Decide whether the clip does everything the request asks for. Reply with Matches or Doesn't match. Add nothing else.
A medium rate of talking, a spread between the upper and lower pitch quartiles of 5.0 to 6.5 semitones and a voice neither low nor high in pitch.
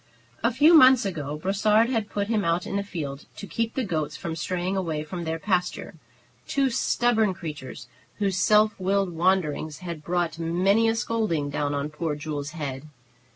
Matches